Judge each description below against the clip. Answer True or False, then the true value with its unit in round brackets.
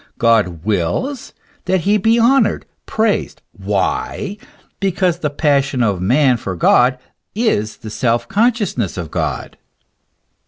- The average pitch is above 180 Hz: False (145 Hz)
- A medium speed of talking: False (120 wpm)